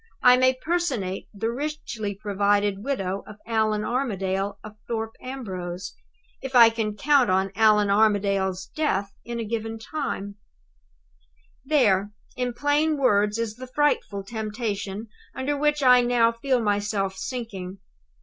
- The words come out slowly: Yes, slow, 130 wpm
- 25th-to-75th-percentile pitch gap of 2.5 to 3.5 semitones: No, average, 4.1 semitones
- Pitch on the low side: No, high, 220 Hz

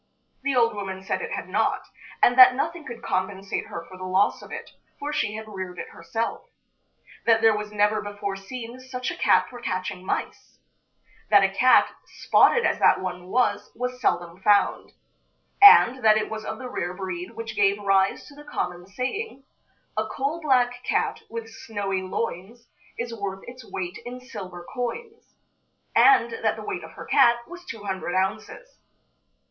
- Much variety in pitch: No, average, 4.7 semitones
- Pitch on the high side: Yes, high, 215 Hz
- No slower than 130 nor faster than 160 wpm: No, average, 175 wpm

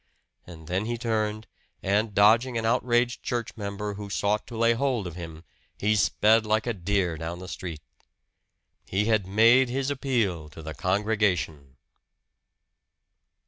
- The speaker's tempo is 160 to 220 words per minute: No, average, 145 wpm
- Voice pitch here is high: No, low, 105 Hz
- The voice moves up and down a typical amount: Yes, average, 4.1 semitones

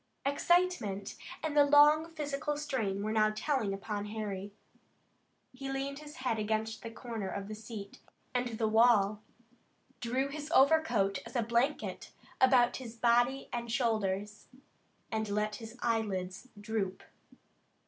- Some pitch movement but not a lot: Yes, average, 4.4 semitones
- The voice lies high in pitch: Yes, high, 230 Hz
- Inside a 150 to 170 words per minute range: No, slow, 135 wpm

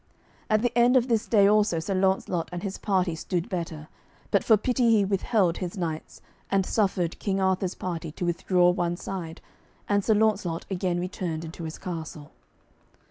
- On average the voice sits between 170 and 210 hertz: Yes, medium, 185 Hz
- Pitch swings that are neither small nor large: Yes, average, 3.2 semitones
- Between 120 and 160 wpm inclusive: No, average, 175 wpm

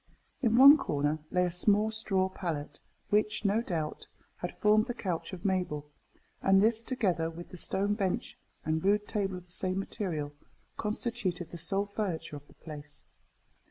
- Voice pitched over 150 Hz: Yes, high, 190 Hz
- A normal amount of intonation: Yes, average, 4.3 semitones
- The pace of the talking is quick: No, average, 165 wpm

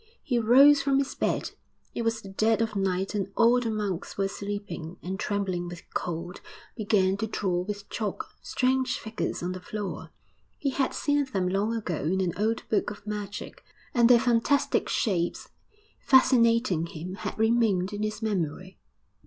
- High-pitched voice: Yes, high, 210 Hz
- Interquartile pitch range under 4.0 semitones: Yes, average, 3.6 semitones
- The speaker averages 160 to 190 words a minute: Yes, average, 170 wpm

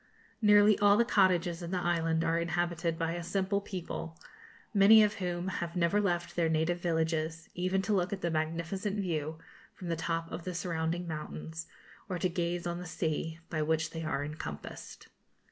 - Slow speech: No, average, 180 wpm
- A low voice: No, medium, 170 Hz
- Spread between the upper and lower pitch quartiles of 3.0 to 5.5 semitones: No, narrow, 2.4 semitones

